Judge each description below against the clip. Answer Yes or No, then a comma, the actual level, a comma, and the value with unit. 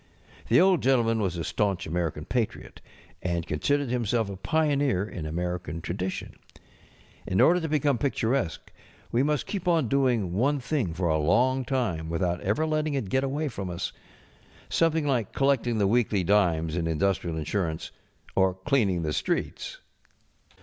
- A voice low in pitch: Yes, low, 110 Hz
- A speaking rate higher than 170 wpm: No, average, 155 wpm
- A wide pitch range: Yes, wide, 7.6 semitones